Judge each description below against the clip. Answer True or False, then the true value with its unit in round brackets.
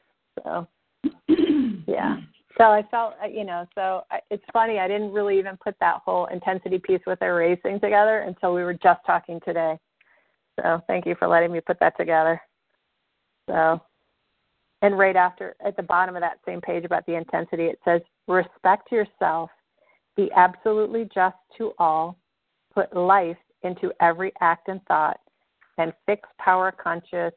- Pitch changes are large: False (3.2 semitones)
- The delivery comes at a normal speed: True (155 wpm)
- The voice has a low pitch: False (185 Hz)